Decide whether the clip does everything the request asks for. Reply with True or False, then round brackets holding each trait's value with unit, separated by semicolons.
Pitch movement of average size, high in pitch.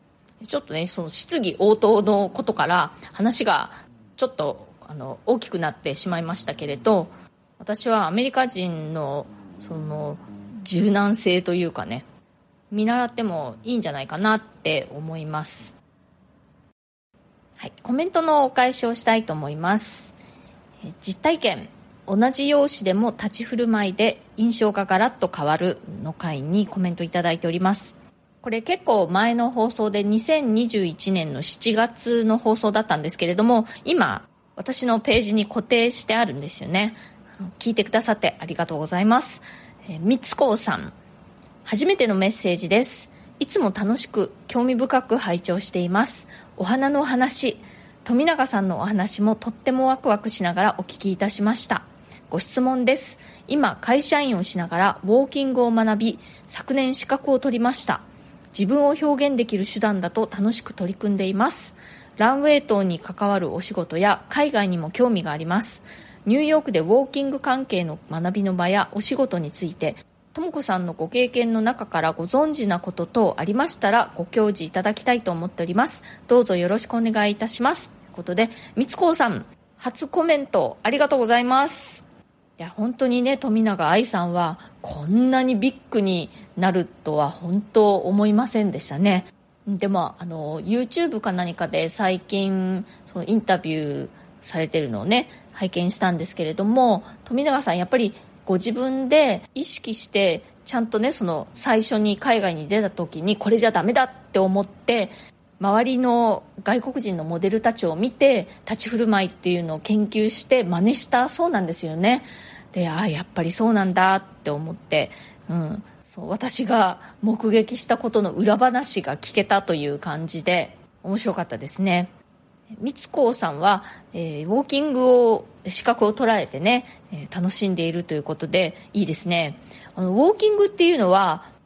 True (5.0 semitones; 210 Hz)